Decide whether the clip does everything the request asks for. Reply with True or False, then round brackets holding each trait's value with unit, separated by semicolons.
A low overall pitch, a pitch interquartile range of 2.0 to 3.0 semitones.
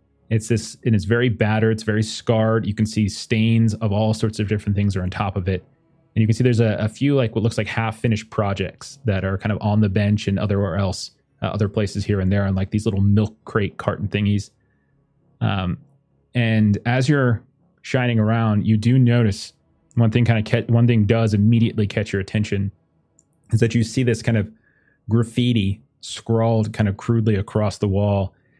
True (110 Hz; 2.4 semitones)